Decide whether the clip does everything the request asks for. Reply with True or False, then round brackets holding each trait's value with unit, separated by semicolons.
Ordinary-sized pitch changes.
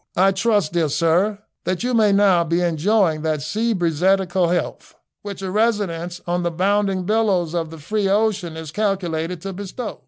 True (3.5 semitones)